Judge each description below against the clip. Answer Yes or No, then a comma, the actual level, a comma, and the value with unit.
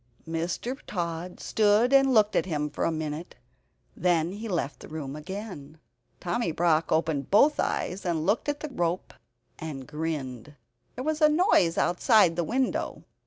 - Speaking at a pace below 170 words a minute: Yes, average, 160 wpm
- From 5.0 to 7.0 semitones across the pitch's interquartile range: Yes, wide, 5.6 semitones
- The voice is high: No, medium, 175 Hz